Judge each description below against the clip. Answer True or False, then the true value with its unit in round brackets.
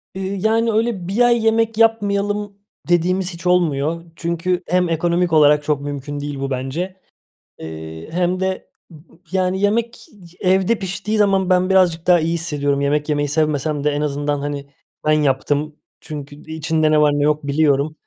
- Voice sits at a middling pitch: True (165 Hz)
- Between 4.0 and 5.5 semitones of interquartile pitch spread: True (4.5 semitones)